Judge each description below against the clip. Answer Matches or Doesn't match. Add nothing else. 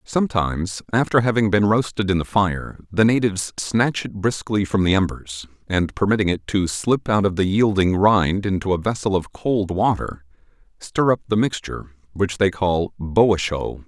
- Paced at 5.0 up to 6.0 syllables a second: Doesn't match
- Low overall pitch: Matches